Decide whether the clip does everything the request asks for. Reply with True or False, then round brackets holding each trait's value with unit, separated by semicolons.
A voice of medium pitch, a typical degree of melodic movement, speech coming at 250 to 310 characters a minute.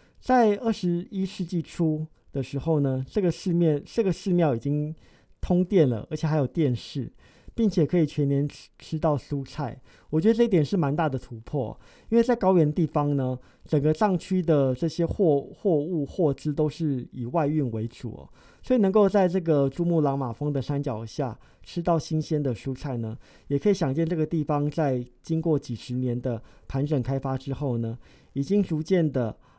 True (150 Hz; 4.1 semitones; 270 characters per minute)